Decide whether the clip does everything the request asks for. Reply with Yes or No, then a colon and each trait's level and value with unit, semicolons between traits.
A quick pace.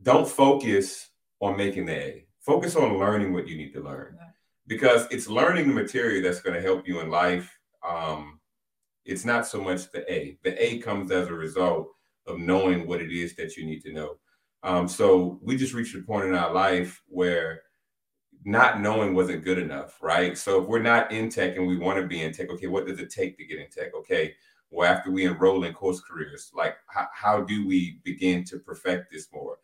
Yes: fast, 215 wpm